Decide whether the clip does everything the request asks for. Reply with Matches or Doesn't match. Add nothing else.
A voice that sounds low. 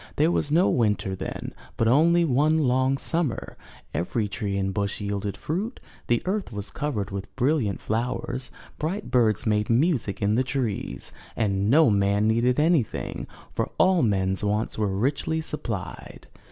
Matches